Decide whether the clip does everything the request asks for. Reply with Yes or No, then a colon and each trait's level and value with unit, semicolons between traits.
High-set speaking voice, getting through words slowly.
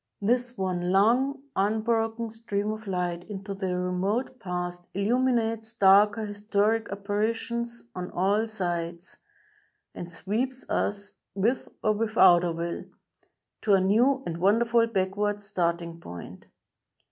Yes: high, 205 Hz; slow, 120 wpm